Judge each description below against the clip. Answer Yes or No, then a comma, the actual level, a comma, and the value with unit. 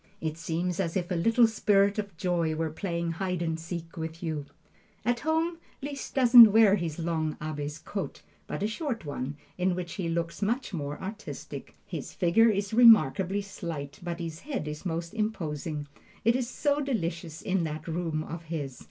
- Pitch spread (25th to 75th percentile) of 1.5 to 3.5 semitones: No, average, 4.8 semitones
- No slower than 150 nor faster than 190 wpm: Yes, average, 180 wpm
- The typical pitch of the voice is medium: Yes, medium, 175 Hz